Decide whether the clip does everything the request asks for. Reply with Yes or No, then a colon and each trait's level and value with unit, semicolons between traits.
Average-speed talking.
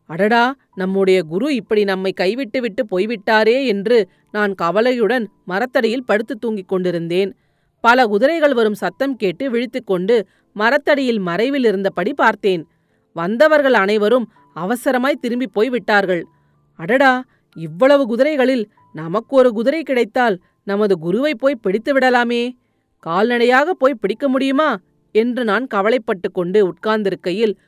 Yes: average, 110 wpm